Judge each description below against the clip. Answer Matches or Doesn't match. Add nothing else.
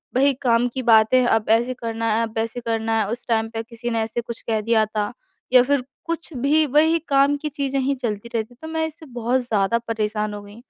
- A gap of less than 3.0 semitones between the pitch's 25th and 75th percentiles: Doesn't match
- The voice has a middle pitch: Doesn't match